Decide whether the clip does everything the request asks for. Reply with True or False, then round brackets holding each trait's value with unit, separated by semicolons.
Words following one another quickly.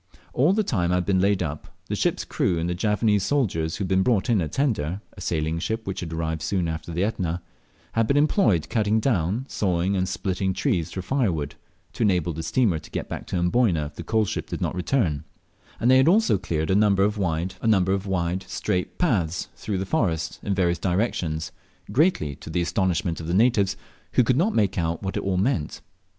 True (215 wpm)